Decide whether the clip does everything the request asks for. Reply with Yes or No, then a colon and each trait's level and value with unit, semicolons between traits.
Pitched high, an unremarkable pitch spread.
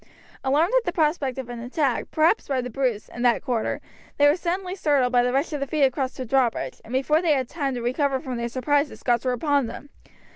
Yes: very high, 270 Hz; average, 3.3 semitones